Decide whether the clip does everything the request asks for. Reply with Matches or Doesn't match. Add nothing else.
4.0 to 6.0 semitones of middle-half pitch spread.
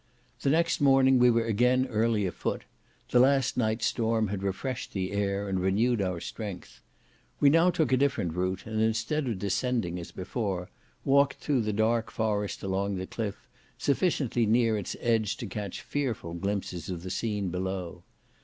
Matches